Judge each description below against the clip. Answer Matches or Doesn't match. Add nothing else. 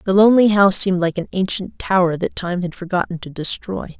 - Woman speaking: Matches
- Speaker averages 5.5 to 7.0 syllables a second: Matches